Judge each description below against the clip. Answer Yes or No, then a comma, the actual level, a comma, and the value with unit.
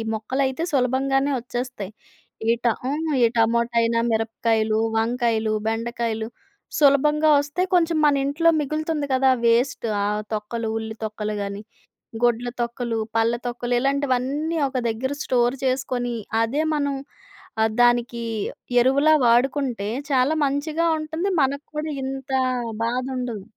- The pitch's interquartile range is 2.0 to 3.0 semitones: No, average, 3.4 semitones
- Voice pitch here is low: No, very high, 250 Hz